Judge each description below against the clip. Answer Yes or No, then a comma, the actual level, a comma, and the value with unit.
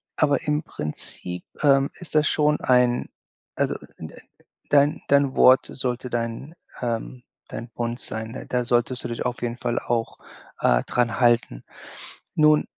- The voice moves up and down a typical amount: Yes, average, 3.1 semitones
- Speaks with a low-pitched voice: Yes, low, 125 Hz